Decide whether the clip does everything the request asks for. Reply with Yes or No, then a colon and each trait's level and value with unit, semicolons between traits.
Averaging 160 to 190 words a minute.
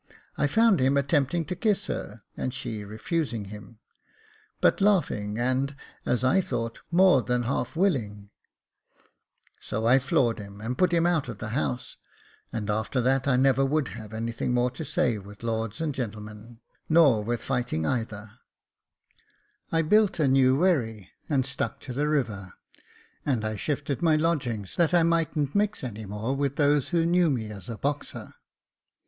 Yes: average, 165 wpm